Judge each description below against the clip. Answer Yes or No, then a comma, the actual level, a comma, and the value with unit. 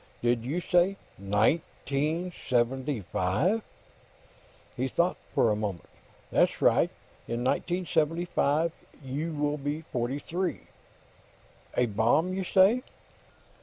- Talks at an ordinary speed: No, slow, 105 wpm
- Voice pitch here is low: No, medium, 145 Hz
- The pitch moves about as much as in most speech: No, wide, 6.3 semitones